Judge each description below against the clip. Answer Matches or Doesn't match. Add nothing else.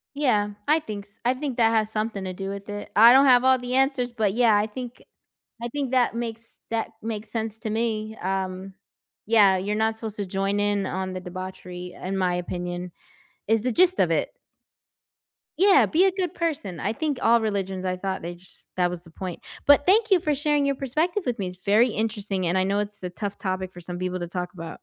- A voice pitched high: Matches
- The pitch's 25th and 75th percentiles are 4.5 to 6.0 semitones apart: Matches